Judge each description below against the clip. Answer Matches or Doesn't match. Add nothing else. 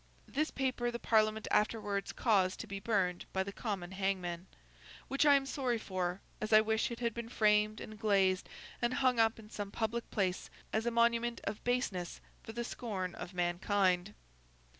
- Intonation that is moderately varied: Matches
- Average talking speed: Matches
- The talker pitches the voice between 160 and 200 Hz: Doesn't match